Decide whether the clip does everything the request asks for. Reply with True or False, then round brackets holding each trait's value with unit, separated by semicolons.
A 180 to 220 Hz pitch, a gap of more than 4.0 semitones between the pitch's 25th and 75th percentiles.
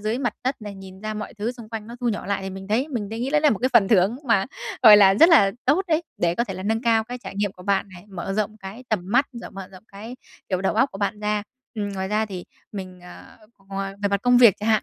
False (210 Hz; 3.4 semitones)